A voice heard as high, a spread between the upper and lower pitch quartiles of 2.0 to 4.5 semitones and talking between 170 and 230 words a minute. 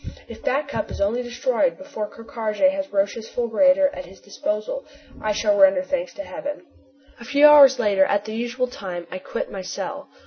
No: very high, 255 Hz; average, 5.2 semitones; average, 195 wpm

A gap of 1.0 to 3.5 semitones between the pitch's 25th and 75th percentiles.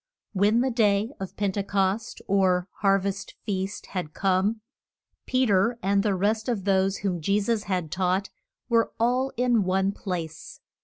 Yes: narrow, 2.5 semitones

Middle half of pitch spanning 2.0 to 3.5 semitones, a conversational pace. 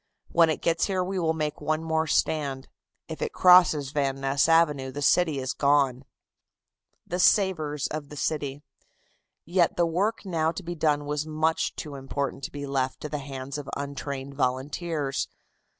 Yes: average, 2.9 semitones; average, 170 wpm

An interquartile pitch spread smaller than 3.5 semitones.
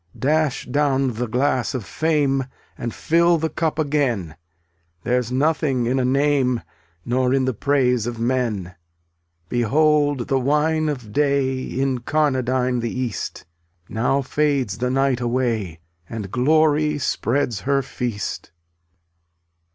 Yes: average, 3.1 semitones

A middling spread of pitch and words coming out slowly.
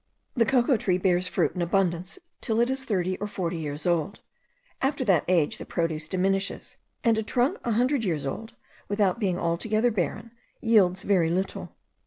No: average, 4.4 semitones; average, 175 wpm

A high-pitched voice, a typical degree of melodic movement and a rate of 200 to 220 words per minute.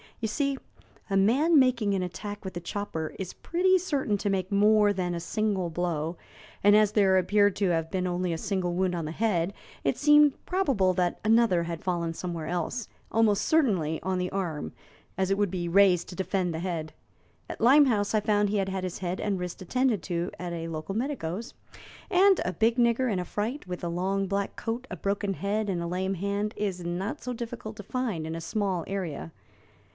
Yes: high, 195 Hz; average, 3.5 semitones; fast, 205 wpm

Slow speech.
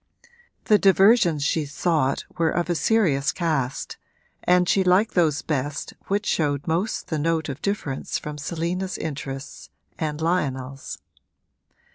Yes: slow, 130 wpm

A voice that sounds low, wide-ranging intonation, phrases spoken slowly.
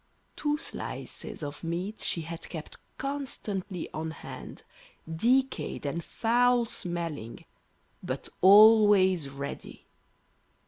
No: medium, 185 Hz; wide, 5.8 semitones; slow, 95 wpm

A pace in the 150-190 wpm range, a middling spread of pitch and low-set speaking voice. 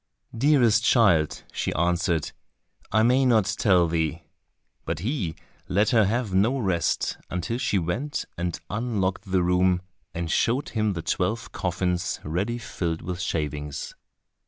No: slow, 135 wpm; average, 4.9 semitones; very low, 95 Hz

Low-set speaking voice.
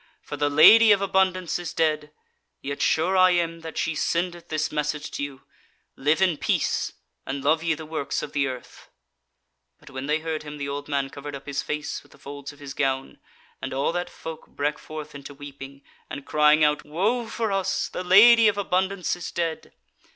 No: medium, 155 Hz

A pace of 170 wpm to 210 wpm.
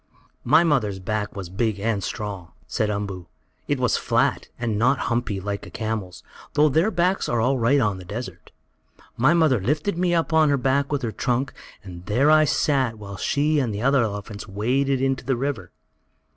Yes: average, 190 wpm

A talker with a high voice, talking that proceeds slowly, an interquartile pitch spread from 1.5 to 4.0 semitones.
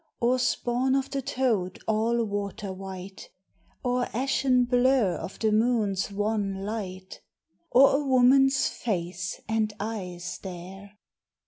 No: high, 220 Hz; slow, 120 wpm; average, 4.5 semitones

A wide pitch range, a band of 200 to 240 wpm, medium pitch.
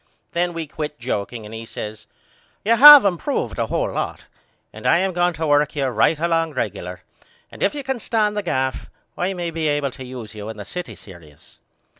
Yes: wide, 7.9 semitones; fast, 205 wpm; medium, 155 Hz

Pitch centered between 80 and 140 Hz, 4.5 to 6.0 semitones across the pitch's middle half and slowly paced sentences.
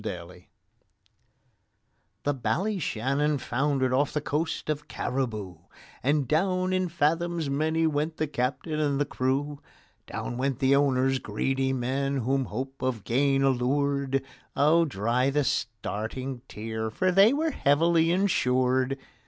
No: low, 135 Hz; average, 3.1 semitones; slow, 120 wpm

